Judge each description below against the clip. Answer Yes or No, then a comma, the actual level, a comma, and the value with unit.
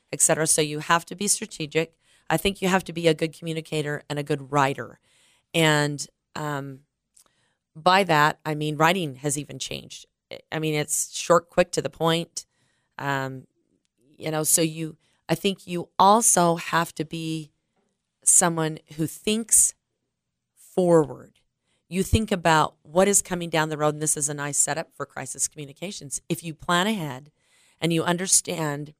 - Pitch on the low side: No, medium, 160 Hz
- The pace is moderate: Yes, average, 165 wpm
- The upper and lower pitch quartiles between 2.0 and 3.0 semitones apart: Yes, narrow, 2.4 semitones